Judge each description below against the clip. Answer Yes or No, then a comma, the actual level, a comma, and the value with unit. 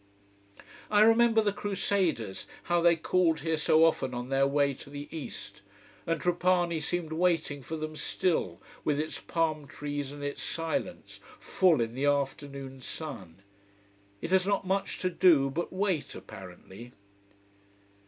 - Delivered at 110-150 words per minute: Yes, average, 145 wpm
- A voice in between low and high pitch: Yes, medium, 155 Hz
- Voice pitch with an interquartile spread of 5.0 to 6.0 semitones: No, average, 4.3 semitones